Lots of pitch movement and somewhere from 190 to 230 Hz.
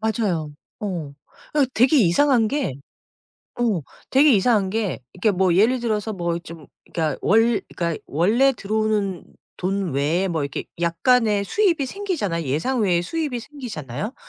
Yes: wide, 6.2 semitones; high, 205 Hz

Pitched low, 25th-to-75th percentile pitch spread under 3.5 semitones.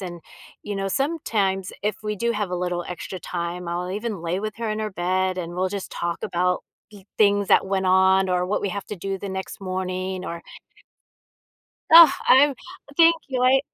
No: high, 190 Hz; narrow, 2.5 semitones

